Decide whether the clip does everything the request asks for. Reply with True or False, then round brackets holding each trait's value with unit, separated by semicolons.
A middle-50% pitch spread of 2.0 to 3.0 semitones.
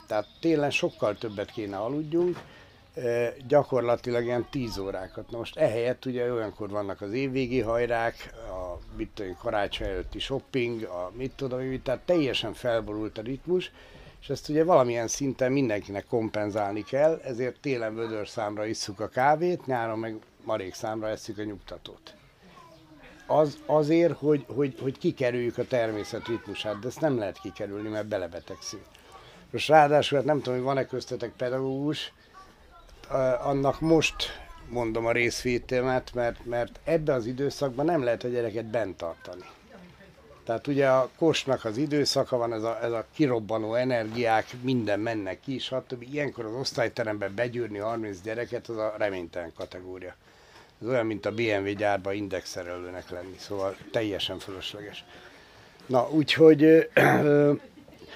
False (3.8 semitones)